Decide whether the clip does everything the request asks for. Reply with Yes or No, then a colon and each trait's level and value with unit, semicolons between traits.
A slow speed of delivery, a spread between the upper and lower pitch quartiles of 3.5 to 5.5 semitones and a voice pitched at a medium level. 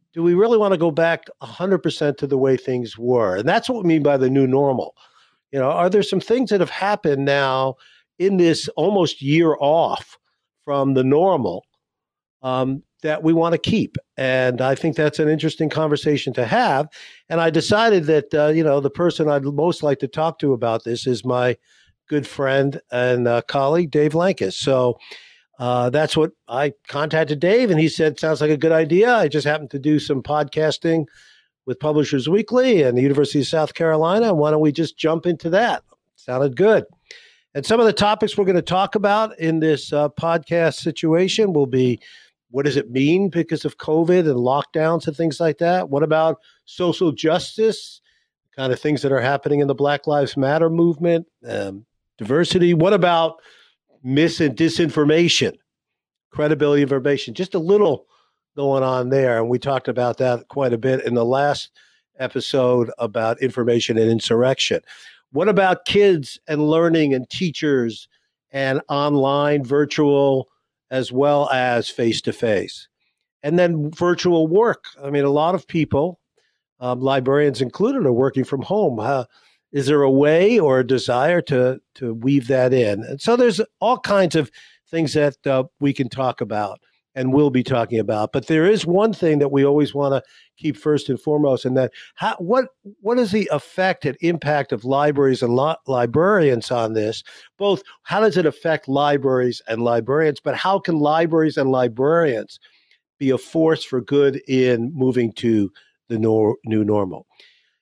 No: average, 180 wpm; average, 4.0 semitones; medium, 145 Hz